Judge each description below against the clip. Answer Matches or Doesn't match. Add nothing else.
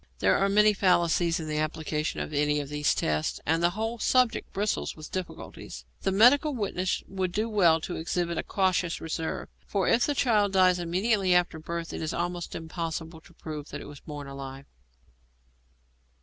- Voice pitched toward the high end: Doesn't match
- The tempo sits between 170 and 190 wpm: Matches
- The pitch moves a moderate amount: Matches